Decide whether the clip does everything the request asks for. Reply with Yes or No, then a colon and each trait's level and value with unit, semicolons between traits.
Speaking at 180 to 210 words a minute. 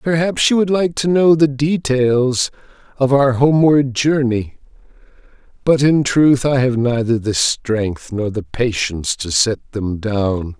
No: average, 155 wpm